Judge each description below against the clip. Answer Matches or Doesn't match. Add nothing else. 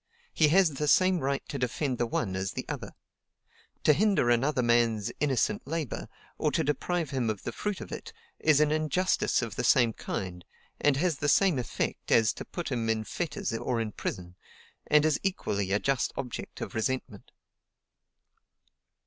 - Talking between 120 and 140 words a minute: Doesn't match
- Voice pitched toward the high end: Doesn't match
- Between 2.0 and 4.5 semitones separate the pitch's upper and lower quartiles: Doesn't match